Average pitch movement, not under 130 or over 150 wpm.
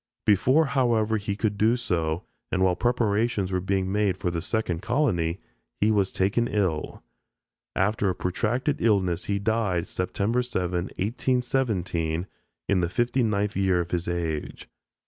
Yes: average, 4.2 semitones; average, 145 wpm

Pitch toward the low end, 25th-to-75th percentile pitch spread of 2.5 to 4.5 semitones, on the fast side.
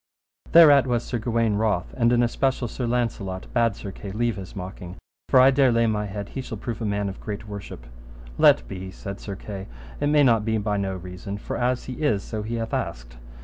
Yes: low, 110 Hz; average, 3.5 semitones; fast, 225 wpm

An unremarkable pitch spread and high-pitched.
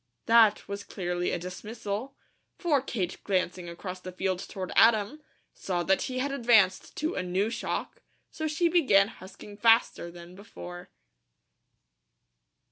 Yes: average, 4.6 semitones; high, 200 Hz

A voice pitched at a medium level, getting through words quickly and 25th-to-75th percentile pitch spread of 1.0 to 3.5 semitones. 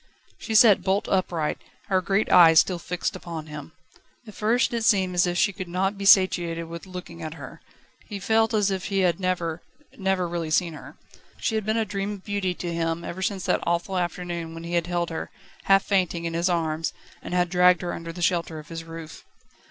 Yes: medium, 180 Hz; fast, 215 wpm; narrow, 2.6 semitones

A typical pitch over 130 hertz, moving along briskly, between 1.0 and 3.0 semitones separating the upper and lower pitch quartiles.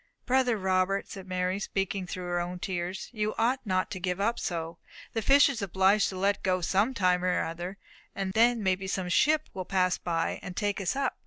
Yes: high, 190 Hz; fast, 215 wpm; narrow, 2.5 semitones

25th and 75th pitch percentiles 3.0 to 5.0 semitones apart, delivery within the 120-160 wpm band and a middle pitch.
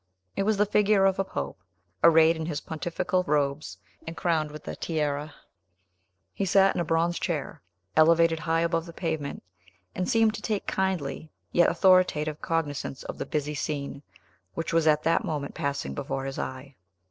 No: average, 3.3 semitones; average, 170 wpm; medium, 160 Hz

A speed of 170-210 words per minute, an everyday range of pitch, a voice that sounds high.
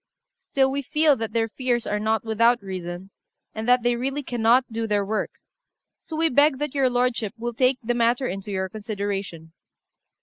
Yes: average, 180 wpm; average, 3.5 semitones; high, 230 Hz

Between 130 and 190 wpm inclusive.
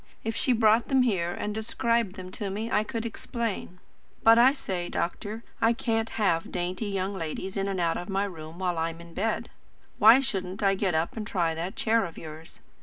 No: fast, 205 wpm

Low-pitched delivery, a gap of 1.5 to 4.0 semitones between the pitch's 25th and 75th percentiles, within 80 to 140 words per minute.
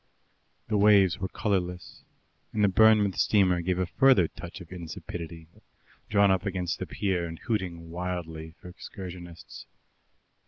Yes: very low, 90 Hz; average, 2.7 semitones; slow, 135 wpm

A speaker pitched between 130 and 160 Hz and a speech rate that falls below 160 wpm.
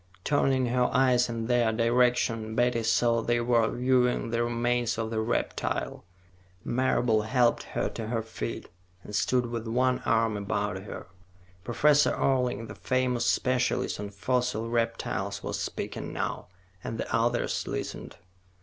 No: low, 120 Hz; average, 140 wpm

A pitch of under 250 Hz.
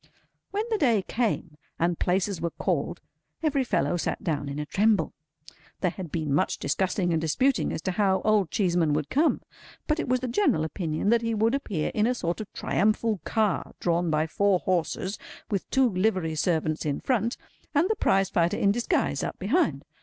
Yes: high, 190 Hz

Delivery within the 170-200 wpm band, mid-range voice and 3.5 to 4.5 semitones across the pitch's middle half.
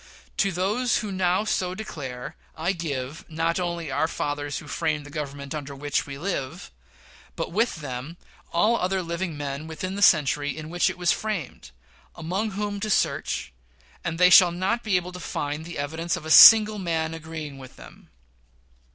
Yes: average, 175 wpm; medium, 165 Hz; average, 4.2 semitones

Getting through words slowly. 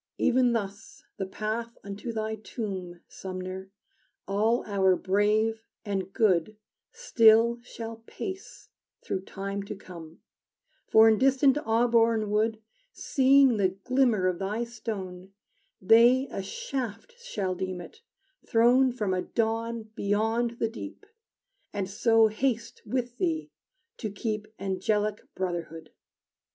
Yes: slow, 120 wpm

